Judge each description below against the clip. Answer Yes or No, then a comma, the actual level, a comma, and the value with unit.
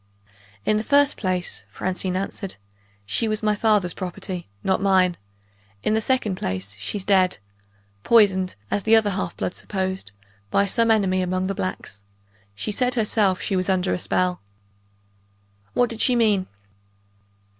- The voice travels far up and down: No, average, 2.8 semitones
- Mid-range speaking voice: No, high, 195 Hz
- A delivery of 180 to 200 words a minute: No, average, 150 wpm